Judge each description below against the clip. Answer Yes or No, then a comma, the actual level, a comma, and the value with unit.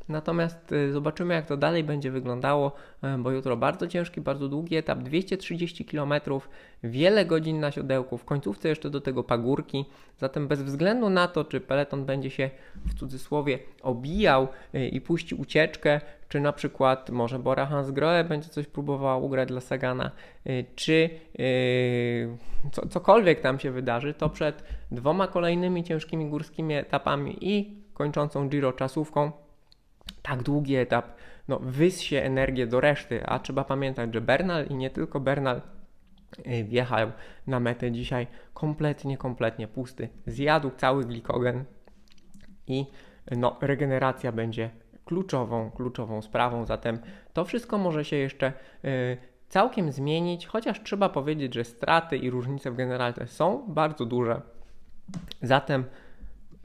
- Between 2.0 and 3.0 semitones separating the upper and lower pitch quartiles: No, average, 3.5 semitones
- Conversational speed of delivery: Yes, average, 135 wpm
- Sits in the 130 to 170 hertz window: Yes, medium, 140 Hz